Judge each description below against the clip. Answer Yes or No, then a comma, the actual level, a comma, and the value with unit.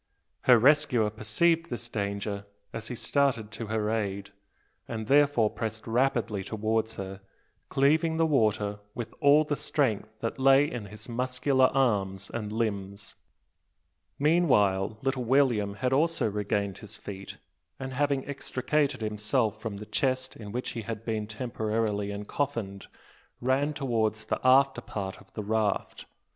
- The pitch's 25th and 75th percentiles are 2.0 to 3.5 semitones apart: No, average, 4.3 semitones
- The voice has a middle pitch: No, low, 115 Hz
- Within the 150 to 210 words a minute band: No, average, 140 wpm